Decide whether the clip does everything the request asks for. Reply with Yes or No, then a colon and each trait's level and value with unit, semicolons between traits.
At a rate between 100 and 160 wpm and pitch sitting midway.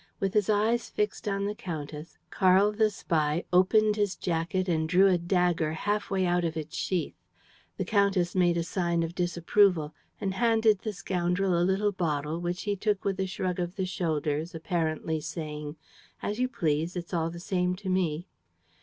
No: average, 180 wpm; medium, 180 Hz